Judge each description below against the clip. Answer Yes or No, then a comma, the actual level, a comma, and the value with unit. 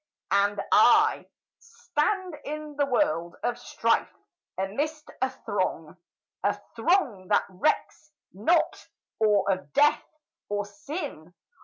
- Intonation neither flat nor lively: No, wide, 7.4 semitones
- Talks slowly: Yes, slow, 110 wpm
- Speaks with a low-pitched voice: No, high, 245 Hz